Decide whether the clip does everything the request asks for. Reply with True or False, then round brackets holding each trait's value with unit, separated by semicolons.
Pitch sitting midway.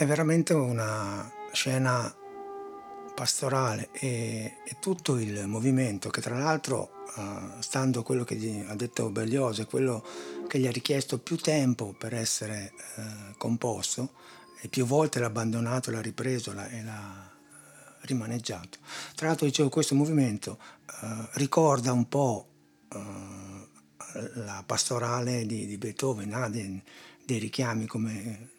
False (120 Hz)